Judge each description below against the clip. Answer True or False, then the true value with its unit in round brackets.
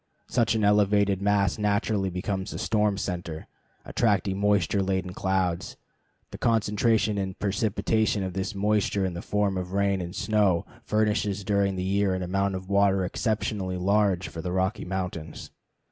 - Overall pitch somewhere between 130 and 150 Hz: False (100 Hz)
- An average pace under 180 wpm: True (155 wpm)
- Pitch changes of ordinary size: False (1.9 semitones)